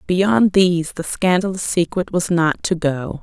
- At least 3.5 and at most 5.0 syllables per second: Yes, 4.2 syllables/s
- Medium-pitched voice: Yes, medium, 175 Hz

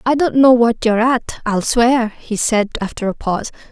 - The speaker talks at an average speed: No, fast, 210 wpm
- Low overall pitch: No, high, 230 Hz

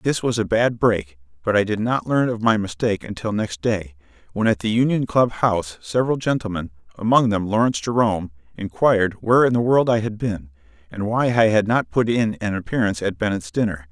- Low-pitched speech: Yes, low, 105 Hz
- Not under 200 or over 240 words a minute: Yes, fast, 205 wpm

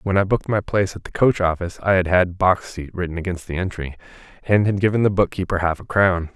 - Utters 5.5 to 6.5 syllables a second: Yes, 6.3 syllables/s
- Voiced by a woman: No, male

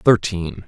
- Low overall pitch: Yes, very low, 95 Hz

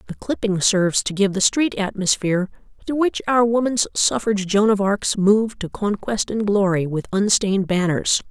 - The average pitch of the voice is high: Yes, high, 205 Hz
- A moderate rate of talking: Yes, average, 175 wpm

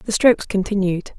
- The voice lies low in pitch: No, high, 200 Hz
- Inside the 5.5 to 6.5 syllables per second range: No, 5.3 syllables/s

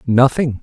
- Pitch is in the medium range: No, low, 130 Hz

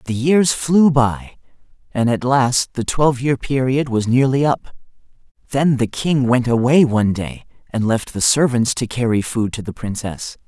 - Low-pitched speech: Yes, low, 125 Hz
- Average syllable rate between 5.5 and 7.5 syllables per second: No, 4.5 syllables/s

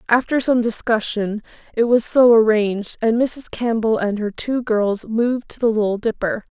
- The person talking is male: No, female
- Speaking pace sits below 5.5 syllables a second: Yes, 4.8 syllables/s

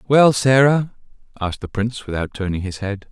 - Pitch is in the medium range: No, low, 115 Hz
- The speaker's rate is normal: Yes, average, 175 wpm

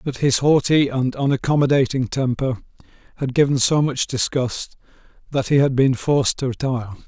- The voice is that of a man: Yes, male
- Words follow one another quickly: No, average, 155 wpm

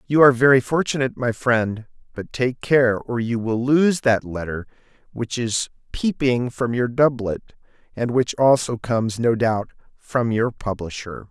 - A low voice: Yes, low, 120 Hz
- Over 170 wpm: No, average, 160 wpm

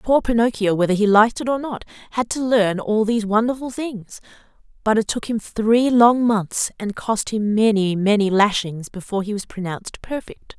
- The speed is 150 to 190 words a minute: Yes, average, 185 wpm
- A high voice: Yes, high, 215 Hz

